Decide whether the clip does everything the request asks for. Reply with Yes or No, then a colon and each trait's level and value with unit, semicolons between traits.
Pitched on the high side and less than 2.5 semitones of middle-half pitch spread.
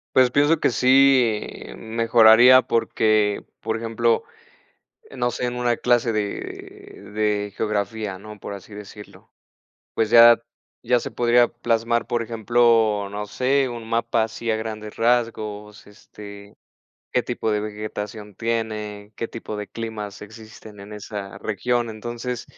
No: low, 110 Hz; narrow, 2.1 semitones